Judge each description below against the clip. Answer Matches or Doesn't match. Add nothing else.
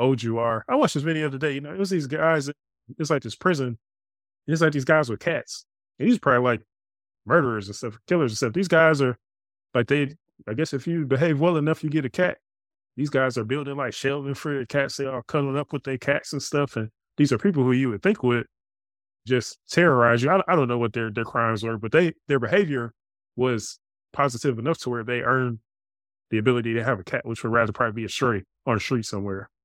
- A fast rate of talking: Matches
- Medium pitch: Doesn't match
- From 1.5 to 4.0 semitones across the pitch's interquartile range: Doesn't match